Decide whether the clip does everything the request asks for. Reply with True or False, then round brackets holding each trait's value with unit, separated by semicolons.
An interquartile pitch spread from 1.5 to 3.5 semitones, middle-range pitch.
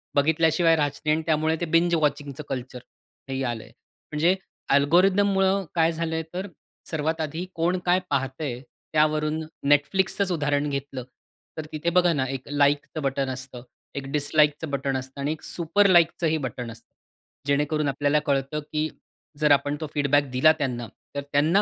True (2.7 semitones; 150 Hz)